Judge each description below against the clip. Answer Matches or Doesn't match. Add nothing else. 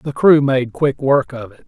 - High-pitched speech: Doesn't match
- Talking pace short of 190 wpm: Doesn't match